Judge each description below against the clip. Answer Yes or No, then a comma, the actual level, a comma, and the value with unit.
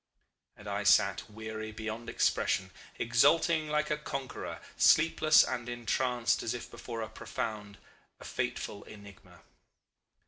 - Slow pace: Yes, slow, 125 wpm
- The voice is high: No, low, 115 Hz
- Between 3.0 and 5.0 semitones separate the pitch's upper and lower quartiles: Yes, average, 4.2 semitones